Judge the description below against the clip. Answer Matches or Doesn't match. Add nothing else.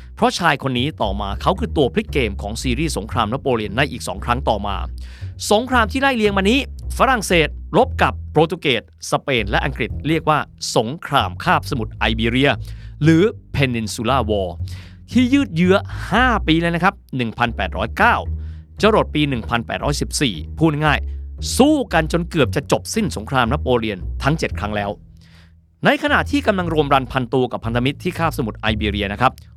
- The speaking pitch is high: Doesn't match